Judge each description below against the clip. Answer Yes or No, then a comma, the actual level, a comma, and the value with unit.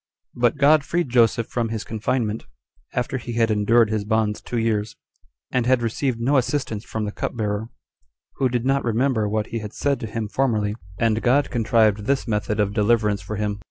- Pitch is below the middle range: Yes, low, 115 Hz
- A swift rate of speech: No, average, 195 wpm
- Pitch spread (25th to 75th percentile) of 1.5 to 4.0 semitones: Yes, average, 2.7 semitones